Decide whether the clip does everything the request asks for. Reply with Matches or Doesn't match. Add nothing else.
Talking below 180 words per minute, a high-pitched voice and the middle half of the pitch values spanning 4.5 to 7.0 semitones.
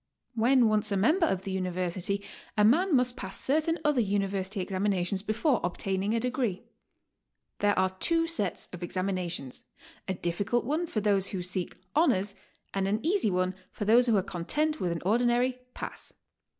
Matches